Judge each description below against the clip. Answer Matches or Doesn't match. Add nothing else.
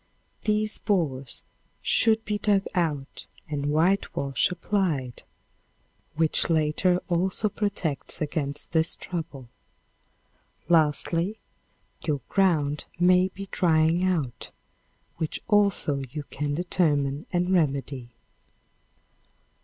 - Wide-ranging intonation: Doesn't match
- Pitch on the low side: Doesn't match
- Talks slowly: Matches